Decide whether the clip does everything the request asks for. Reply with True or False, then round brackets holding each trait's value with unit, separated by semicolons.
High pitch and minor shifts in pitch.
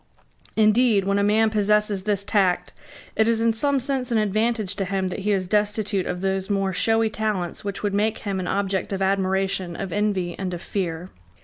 True (200 Hz; 2.2 semitones)